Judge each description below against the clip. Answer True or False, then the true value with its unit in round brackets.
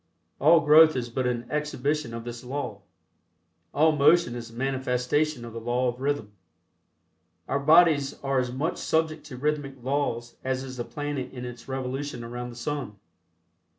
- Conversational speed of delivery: True (165 wpm)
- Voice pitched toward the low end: True (130 Hz)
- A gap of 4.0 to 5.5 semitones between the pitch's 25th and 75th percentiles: False (3.3 semitones)